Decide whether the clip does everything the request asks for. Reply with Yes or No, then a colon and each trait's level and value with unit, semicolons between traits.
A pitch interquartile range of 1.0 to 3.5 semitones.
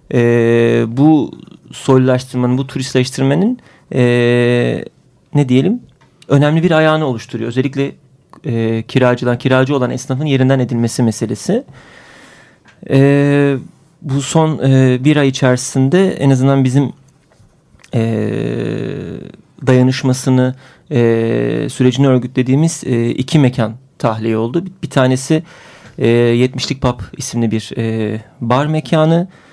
Yes: average, 2.7 semitones